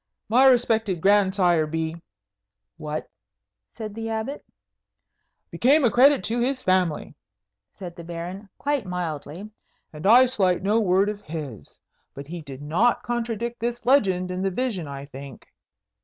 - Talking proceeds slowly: No, average, 145 wpm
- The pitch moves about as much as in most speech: No, wide, 6.3 semitones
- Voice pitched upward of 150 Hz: Yes, high, 190 Hz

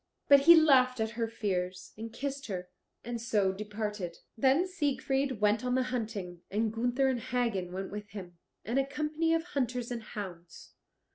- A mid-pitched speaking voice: No, high, 230 Hz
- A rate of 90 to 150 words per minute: No, average, 170 wpm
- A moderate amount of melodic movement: Yes, average, 4.6 semitones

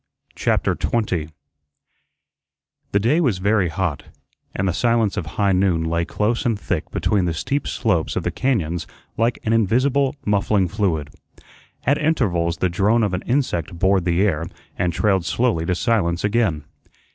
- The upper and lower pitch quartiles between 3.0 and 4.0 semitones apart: No, average, 4.9 semitones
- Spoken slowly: No, average, 160 wpm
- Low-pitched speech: Yes, low, 100 Hz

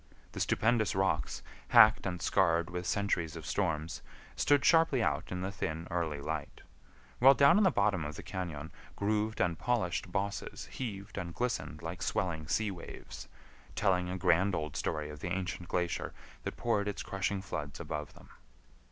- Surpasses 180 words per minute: No, average, 170 wpm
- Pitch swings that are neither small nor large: Yes, average, 4.0 semitones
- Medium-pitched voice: No, very low, 90 Hz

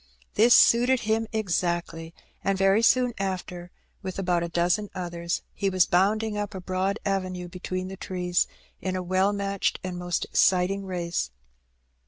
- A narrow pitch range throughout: Yes, narrow, 2.0 semitones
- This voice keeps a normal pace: Yes, average, 155 wpm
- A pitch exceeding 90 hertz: Yes, medium, 185 Hz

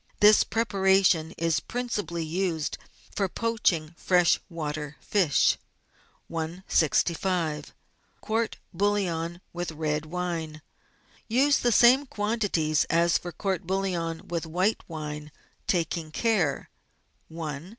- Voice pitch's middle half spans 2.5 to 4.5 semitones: Yes, average, 3.8 semitones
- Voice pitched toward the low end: No, medium, 170 Hz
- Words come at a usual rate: No, slow, 105 wpm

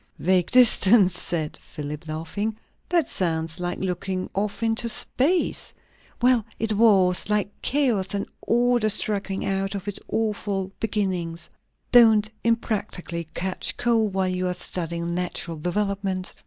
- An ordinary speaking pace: No, slow, 130 wpm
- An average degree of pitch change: Yes, average, 3.6 semitones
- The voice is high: Yes, high, 195 Hz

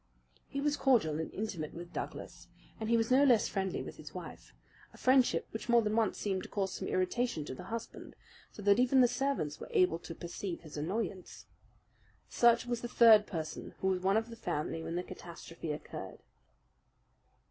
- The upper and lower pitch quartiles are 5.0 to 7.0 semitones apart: Yes, wide, 5.5 semitones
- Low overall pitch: No, high, 205 Hz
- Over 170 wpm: Yes, average, 190 wpm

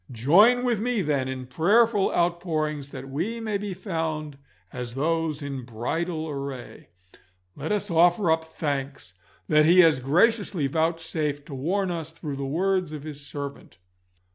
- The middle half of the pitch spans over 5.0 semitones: No, average, 4.4 semitones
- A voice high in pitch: No, medium, 160 Hz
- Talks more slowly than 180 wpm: Yes, average, 150 wpm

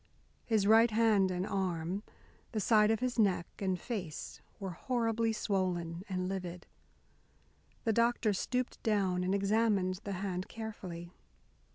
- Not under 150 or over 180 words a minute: No, slow, 135 wpm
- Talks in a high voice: Yes, high, 200 Hz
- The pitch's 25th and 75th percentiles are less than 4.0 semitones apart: Yes, average, 3.4 semitones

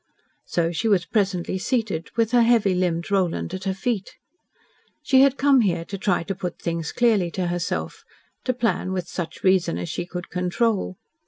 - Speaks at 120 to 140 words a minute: No, average, 180 wpm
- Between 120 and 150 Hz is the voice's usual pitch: No, high, 190 Hz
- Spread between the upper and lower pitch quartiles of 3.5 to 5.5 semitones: Yes, average, 4.4 semitones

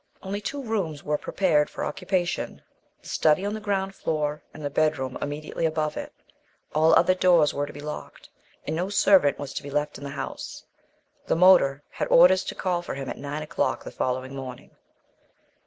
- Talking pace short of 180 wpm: No, average, 190 wpm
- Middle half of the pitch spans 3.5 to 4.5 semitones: Yes, average, 4.2 semitones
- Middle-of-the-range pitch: Yes, medium, 155 Hz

